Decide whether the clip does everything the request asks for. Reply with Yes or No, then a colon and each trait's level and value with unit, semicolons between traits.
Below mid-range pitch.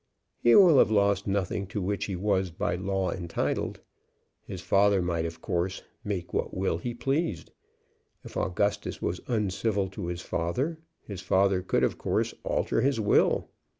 Yes: very low, 95 Hz